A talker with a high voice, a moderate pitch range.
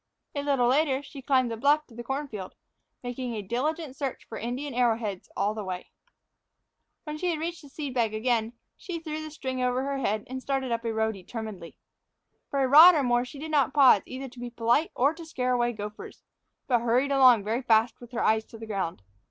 Yes: very high, 250 Hz; average, 3.8 semitones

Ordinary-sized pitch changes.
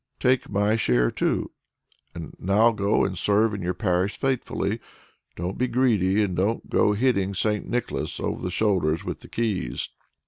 Yes: average, 3.6 semitones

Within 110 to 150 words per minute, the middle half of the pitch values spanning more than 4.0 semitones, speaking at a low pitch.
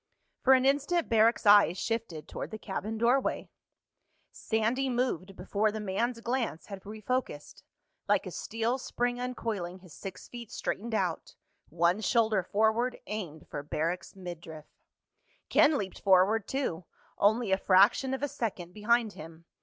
No: average, 140 wpm; average, 4.4 semitones; high, 215 Hz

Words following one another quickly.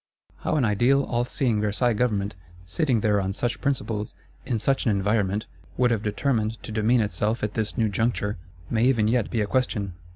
No: average, 190 wpm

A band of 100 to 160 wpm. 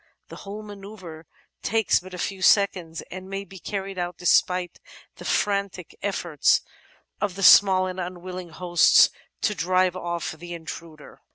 Yes: average, 150 wpm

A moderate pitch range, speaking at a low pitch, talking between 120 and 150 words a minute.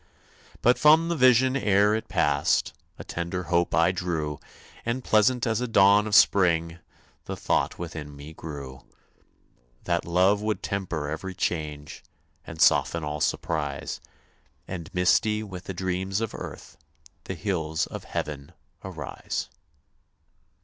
Yes: average, 4.8 semitones; very low, 90 Hz; slow, 135 wpm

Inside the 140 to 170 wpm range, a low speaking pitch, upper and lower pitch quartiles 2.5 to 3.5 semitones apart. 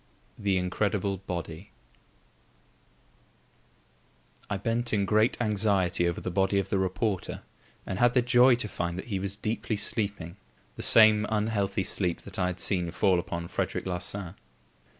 Yes: average, 150 wpm; low, 100 Hz; average, 2.8 semitones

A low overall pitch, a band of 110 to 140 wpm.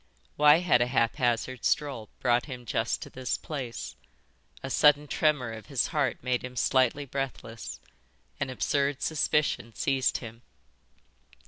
Yes: low, 130 Hz; slow, 135 wpm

